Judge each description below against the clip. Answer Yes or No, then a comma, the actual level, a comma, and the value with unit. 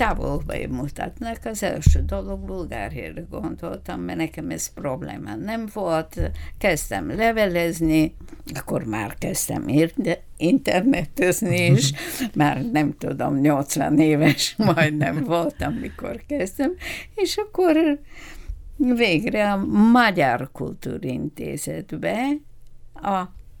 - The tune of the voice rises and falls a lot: Yes, wide, 8.2 semitones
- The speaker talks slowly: Yes, slow, 95 wpm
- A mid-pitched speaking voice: Yes, medium, 160 Hz